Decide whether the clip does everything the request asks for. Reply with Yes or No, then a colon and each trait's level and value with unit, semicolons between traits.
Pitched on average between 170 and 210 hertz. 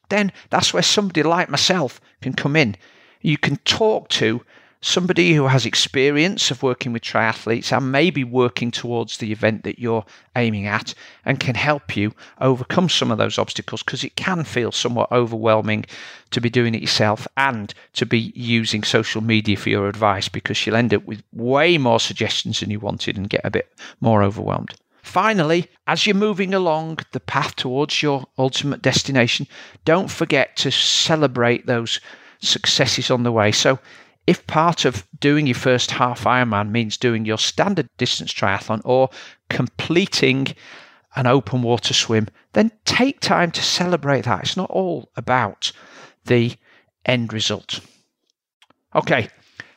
No: low, 125 Hz